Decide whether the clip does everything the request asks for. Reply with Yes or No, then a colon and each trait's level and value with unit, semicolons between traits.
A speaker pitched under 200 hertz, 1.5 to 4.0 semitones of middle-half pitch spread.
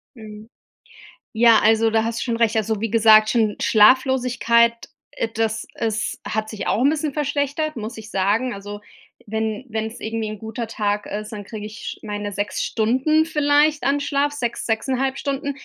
No: high, 225 Hz; average, 3.5 semitones